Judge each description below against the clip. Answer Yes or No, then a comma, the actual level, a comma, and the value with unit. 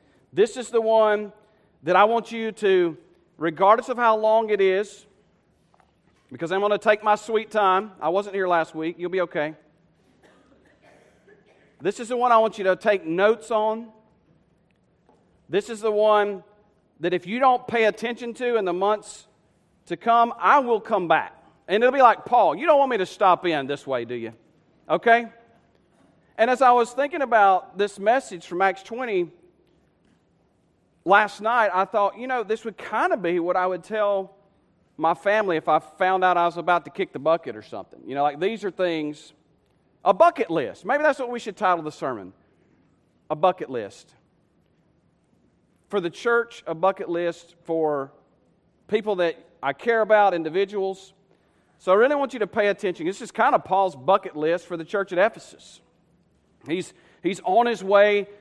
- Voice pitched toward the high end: Yes, high, 200 Hz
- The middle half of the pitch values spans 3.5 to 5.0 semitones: Yes, average, 4.2 semitones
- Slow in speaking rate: No, average, 185 wpm